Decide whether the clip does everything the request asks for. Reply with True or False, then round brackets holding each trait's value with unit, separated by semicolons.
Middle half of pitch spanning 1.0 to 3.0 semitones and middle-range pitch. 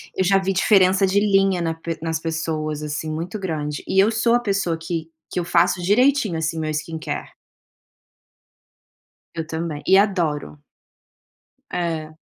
False (3.4 semitones; 170 Hz)